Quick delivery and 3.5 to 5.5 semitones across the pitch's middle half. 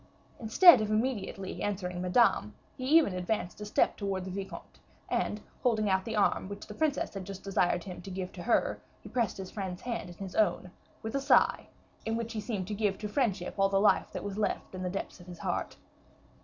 No: fast, 215 wpm; average, 3.0 semitones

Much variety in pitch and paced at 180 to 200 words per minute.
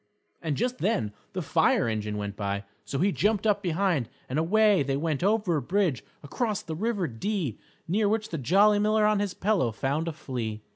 Yes: wide, 7.6 semitones; average, 195 wpm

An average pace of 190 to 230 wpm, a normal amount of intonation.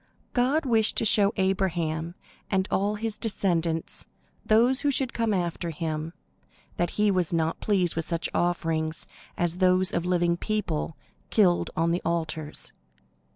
No: average, 145 wpm; average, 4.0 semitones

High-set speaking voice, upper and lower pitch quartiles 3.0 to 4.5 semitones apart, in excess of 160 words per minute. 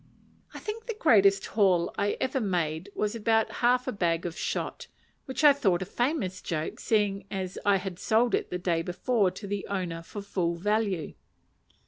Yes: high, 200 Hz; average, 3.9 semitones; average, 180 wpm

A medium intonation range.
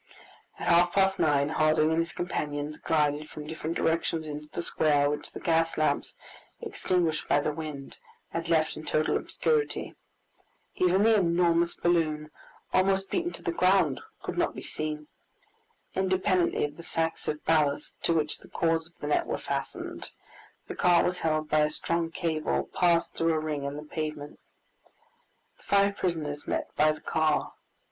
No: narrow, 2.2 semitones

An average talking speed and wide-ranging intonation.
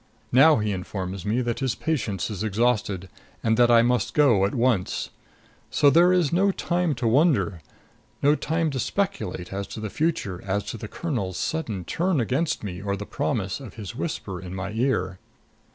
Yes: average, 185 wpm; wide, 7.1 semitones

